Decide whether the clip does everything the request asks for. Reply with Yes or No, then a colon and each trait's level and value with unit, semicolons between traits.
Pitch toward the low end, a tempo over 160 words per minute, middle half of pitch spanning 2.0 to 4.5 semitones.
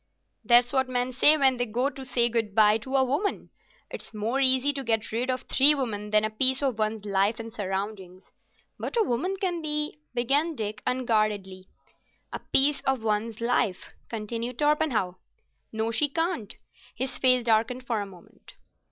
No: high, 240 Hz; average, 180 wpm; average, 3.9 semitones